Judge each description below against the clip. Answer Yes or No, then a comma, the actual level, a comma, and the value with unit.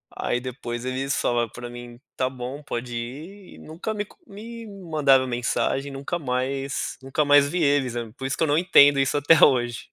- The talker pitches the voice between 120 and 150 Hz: Yes, low, 135 Hz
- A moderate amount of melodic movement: Yes, average, 3.8 semitones